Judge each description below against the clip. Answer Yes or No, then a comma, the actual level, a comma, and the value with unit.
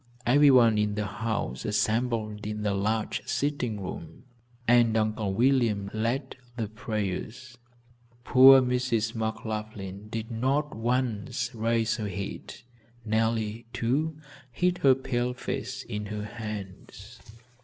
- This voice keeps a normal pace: No, slow, 115 wpm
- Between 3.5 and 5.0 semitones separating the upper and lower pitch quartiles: No, average, 2.8 semitones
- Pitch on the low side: Yes, low, 115 Hz